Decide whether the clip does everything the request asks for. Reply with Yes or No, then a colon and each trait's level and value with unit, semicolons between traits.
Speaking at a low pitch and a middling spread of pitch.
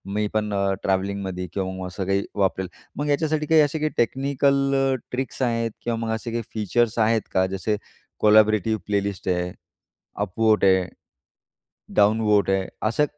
Yes: low, 105 Hz; average, 3.6 semitones